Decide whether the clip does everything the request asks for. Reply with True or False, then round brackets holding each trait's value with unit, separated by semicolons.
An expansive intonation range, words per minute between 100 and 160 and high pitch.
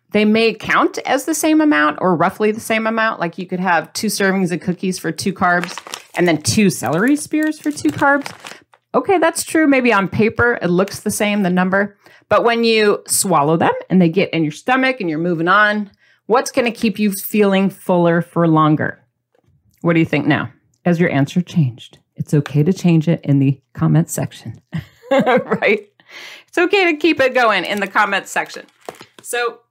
False (6.0 semitones; 195 wpm; 195 Hz)